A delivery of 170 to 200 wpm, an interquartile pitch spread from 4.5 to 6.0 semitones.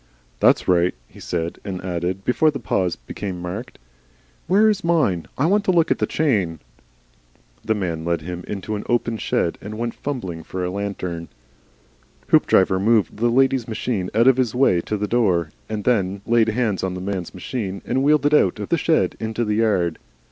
Yes: average, 190 wpm; average, 5.1 semitones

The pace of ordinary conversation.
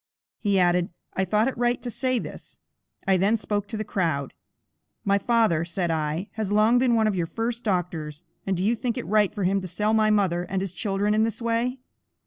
No: fast, 220 wpm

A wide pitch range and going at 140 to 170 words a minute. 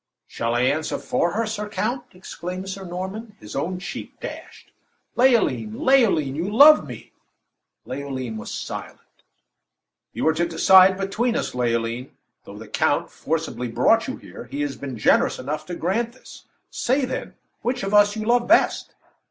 Yes: wide, 7.7 semitones; average, 160 wpm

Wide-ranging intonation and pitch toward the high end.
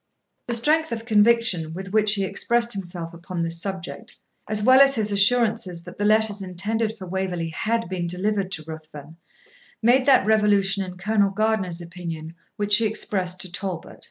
No: average, 3.7 semitones; high, 200 Hz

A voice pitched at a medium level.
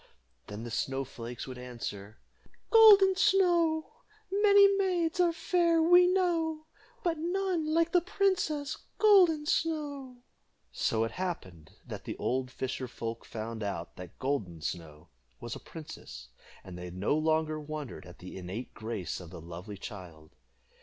Yes: medium, 155 Hz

